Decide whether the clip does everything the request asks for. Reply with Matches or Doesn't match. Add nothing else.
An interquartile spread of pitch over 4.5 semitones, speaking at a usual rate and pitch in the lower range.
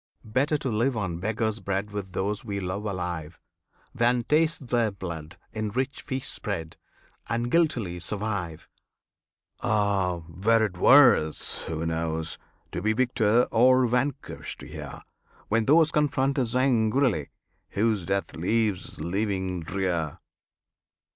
Doesn't match